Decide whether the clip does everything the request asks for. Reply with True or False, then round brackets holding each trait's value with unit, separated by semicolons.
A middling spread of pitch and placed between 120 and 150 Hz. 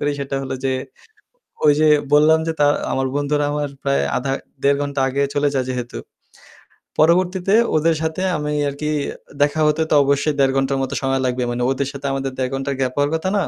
False (2.0 semitones; 140 Hz)